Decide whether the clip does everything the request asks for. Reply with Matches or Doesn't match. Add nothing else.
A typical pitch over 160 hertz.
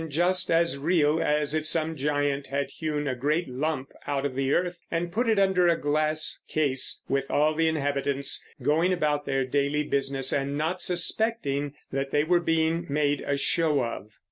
Doesn't match